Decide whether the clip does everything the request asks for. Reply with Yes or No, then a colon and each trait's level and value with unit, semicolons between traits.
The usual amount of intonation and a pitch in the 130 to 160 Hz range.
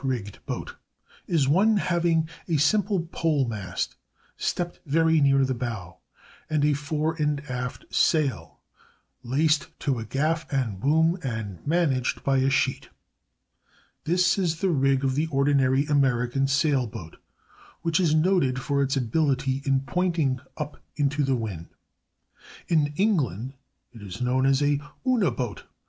Yes: average, 3.8 semitones; medium, 140 Hz